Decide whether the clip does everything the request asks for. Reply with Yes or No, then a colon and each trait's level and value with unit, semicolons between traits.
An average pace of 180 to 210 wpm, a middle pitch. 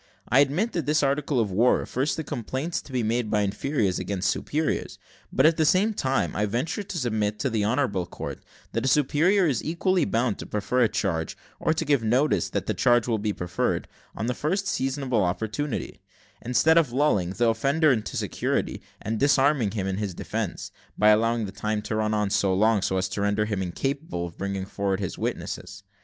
No: average, 200 wpm; low, 115 Hz